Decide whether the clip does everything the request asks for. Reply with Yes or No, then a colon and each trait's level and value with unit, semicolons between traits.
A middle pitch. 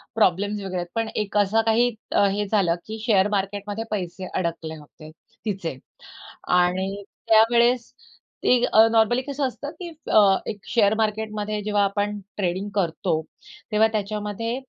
No: high, 205 Hz